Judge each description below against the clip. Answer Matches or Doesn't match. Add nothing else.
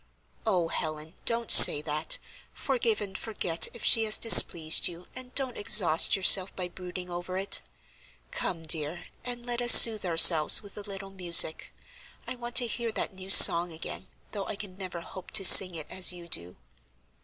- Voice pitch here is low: Doesn't match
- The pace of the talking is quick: Doesn't match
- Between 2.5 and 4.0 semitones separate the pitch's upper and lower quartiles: Doesn't match